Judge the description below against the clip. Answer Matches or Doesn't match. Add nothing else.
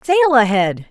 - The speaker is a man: Doesn't match